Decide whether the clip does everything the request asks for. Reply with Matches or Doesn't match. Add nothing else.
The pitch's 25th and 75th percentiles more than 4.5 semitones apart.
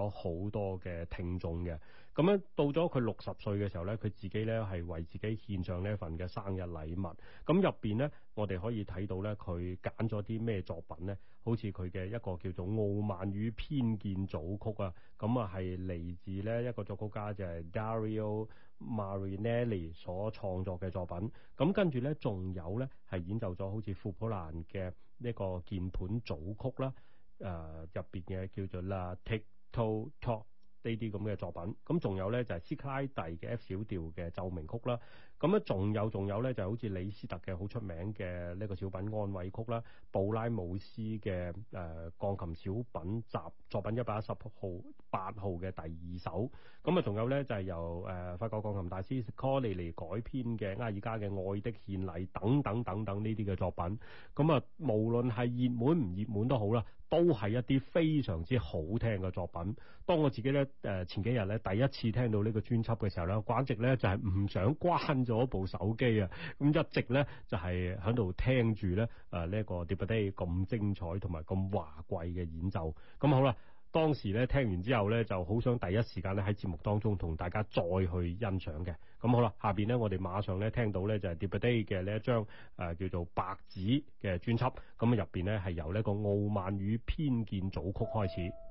Doesn't match